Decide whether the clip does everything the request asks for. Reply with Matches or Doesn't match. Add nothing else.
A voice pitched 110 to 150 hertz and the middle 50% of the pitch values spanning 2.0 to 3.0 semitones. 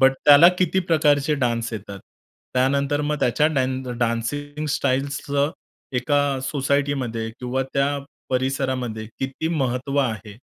Matches